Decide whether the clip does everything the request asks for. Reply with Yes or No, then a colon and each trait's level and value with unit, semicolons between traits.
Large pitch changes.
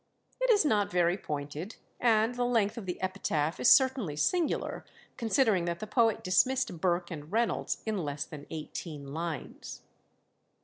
Yes: wide, 6.5 semitones